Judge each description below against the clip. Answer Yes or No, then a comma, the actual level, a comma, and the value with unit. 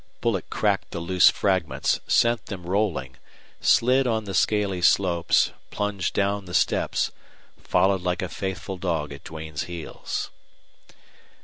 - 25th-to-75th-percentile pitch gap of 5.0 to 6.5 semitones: No, average, 3.1 semitones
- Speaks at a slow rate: Yes, slow, 130 wpm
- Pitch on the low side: Yes, very low, 95 Hz